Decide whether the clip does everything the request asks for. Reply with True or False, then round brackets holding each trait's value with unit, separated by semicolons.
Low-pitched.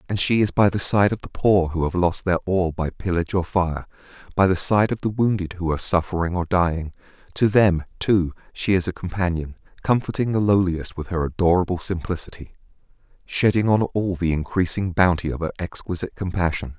True (90 Hz)